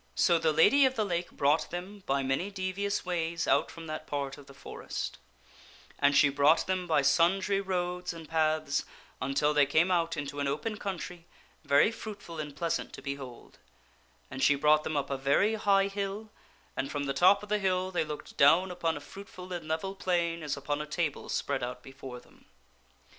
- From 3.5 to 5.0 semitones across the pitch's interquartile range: Yes, average, 4.7 semitones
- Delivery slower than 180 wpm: No, average, 195 wpm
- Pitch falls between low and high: Yes, medium, 165 Hz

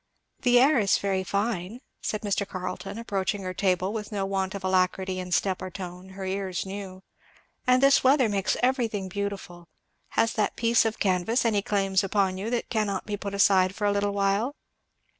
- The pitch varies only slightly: Yes, narrow, 2.3 semitones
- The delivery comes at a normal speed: Yes, average, 180 wpm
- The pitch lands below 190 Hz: No, high, 200 Hz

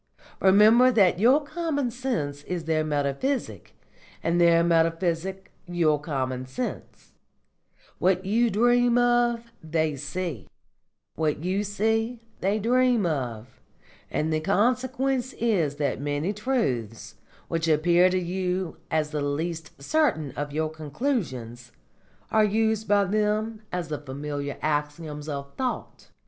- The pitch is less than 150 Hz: No, medium, 175 Hz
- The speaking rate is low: Yes, slow, 125 wpm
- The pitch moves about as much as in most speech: No, wide, 7.0 semitones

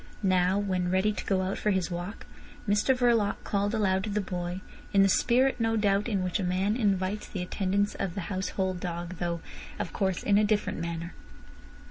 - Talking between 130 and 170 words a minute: No, average, 195 wpm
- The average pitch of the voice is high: Yes, high, 195 Hz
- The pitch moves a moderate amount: No, narrow, 2.3 semitones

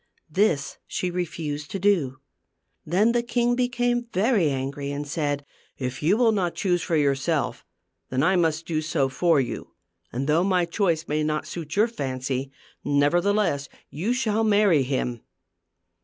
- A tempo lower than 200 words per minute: Yes, average, 155 wpm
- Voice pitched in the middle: Yes, medium, 165 Hz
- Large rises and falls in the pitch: Yes, wide, 6.2 semitones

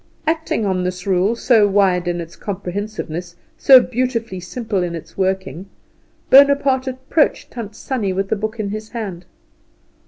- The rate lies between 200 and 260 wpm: No, average, 150 wpm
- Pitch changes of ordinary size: Yes, average, 4.6 semitones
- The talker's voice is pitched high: Yes, high, 205 Hz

